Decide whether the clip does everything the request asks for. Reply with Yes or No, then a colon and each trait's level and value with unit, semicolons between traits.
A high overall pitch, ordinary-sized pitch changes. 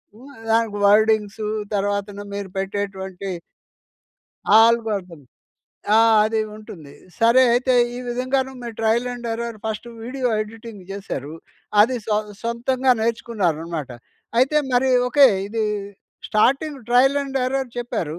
Yes: high, 225 Hz; average, 3.7 semitones